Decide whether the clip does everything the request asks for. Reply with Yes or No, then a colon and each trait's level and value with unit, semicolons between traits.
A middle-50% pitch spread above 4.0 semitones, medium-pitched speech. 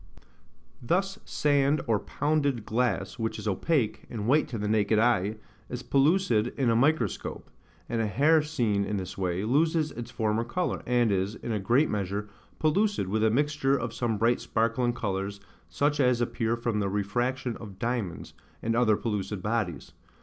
No: average, 4.5 semitones; low, 115 Hz